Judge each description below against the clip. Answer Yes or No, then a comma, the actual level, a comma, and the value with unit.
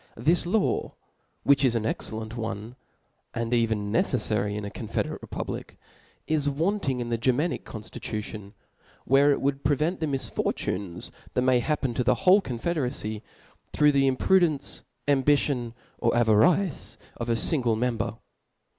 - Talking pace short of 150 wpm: Yes, average, 140 wpm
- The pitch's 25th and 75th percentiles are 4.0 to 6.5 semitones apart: Yes, average, 4.5 semitones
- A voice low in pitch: Yes, low, 125 Hz